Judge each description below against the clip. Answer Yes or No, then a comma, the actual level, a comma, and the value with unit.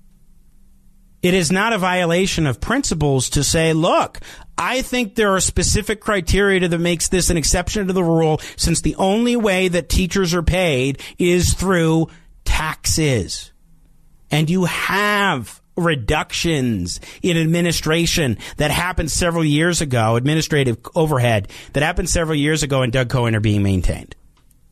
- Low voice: No, medium, 165 Hz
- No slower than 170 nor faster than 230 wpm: No, average, 145 wpm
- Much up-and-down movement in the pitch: Yes, wide, 5.7 semitones